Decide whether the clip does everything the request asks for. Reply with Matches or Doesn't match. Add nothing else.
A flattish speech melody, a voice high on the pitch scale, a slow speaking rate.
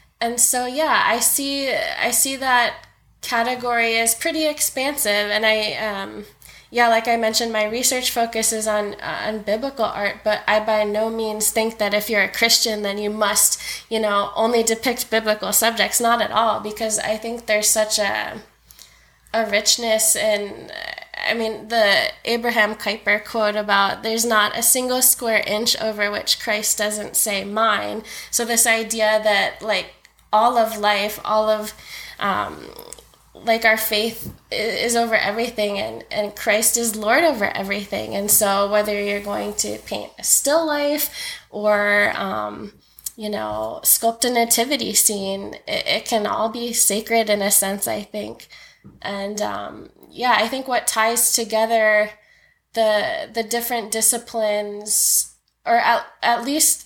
Doesn't match